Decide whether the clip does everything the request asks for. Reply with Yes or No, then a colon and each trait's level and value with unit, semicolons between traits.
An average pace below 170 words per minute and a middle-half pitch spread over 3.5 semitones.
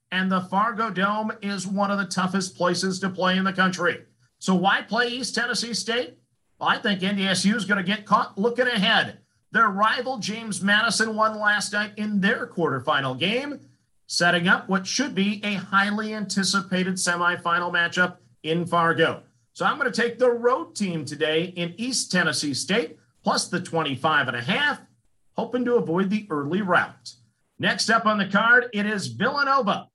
No: average, 175 wpm; average, 4.0 semitones